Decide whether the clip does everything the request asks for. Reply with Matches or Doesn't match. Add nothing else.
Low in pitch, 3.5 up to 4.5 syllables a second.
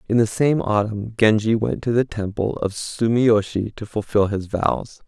Matches